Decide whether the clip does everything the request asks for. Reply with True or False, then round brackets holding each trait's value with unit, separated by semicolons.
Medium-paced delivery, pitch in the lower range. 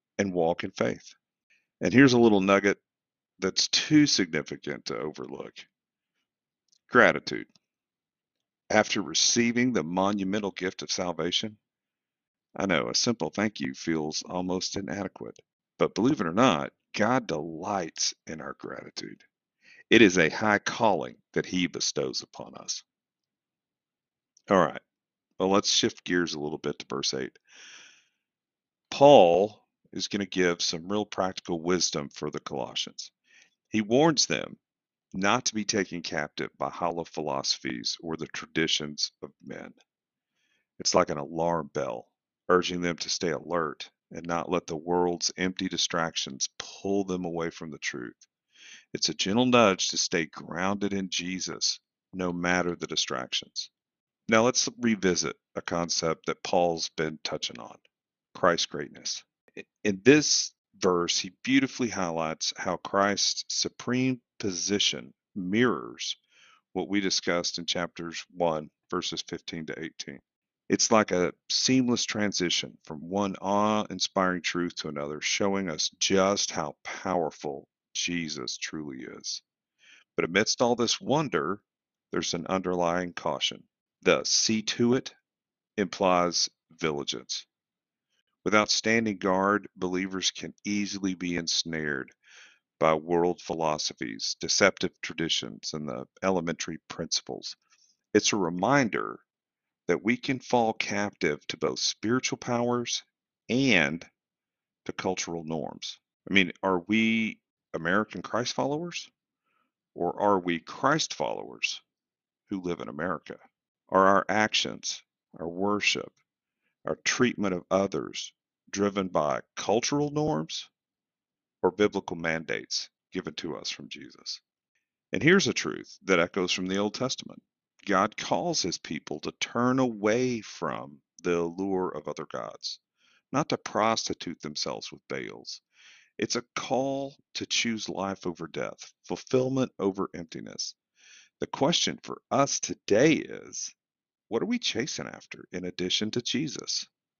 False (130 wpm; 95 Hz)